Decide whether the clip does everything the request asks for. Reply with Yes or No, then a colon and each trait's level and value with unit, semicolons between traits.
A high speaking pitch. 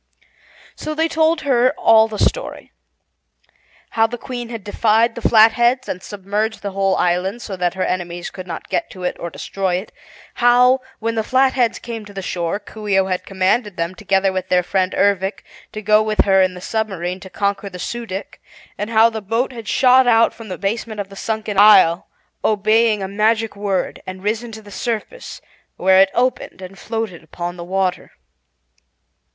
Yes: high, 210 Hz